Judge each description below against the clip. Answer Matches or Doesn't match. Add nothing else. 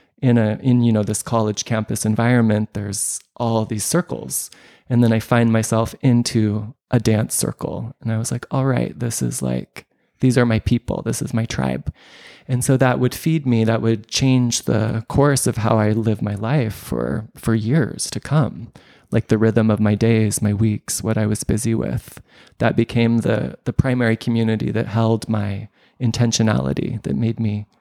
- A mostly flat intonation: Matches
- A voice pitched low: Matches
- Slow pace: Doesn't match